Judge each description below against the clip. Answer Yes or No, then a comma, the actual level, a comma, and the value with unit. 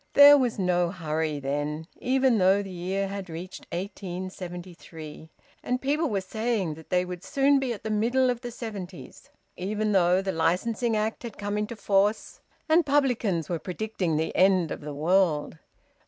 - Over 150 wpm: Yes, average, 170 wpm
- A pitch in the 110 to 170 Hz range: No, high, 195 Hz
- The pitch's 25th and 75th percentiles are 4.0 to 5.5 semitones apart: Yes, average, 4.6 semitones